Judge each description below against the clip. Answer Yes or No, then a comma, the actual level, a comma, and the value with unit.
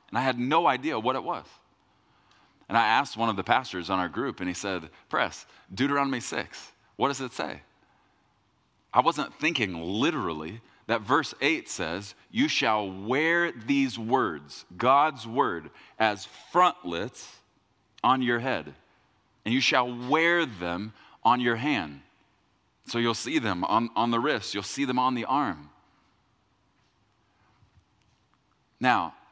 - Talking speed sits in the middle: Yes, average, 145 wpm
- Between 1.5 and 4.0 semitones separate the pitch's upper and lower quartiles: No, average, 4.6 semitones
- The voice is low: Yes, low, 115 Hz